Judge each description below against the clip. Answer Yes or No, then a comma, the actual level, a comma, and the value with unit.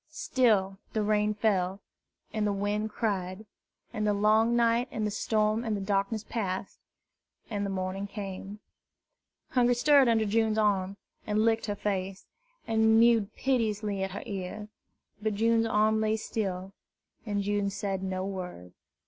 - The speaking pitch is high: Yes, high, 210 Hz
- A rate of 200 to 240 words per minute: No, average, 150 wpm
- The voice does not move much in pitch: Yes, narrow, 2.1 semitones